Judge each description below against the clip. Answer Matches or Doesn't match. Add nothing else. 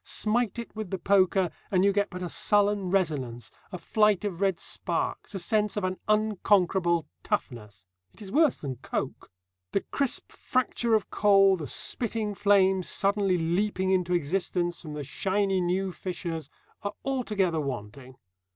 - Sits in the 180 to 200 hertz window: Matches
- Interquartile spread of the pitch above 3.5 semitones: Doesn't match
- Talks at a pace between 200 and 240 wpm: Doesn't match